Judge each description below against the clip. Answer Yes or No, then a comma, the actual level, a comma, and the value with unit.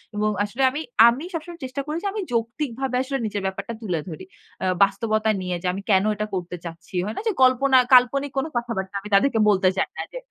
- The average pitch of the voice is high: Yes, high, 225 Hz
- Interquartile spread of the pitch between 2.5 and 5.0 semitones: No, wide, 5.5 semitones